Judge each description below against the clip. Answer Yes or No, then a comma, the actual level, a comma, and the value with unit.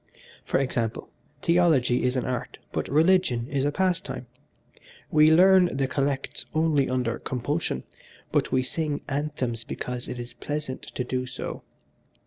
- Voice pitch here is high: No, low, 135 Hz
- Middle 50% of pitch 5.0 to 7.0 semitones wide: No, average, 3.8 semitones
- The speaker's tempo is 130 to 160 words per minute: Yes, average, 140 wpm